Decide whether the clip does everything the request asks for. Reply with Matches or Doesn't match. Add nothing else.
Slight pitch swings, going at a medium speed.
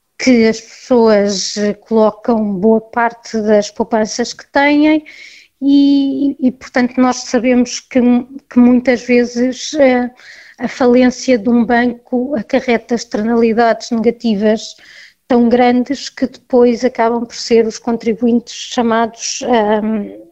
Doesn't match